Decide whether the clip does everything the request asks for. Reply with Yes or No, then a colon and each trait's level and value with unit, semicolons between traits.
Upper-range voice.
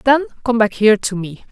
Yes: high, 230 Hz